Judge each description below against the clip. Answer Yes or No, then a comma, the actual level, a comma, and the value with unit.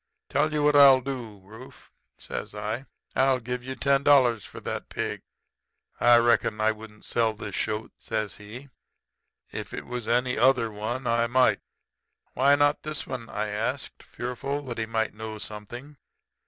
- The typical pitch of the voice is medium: No, low, 120 Hz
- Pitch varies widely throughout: No, average, 3.3 semitones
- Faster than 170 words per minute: No, average, 165 wpm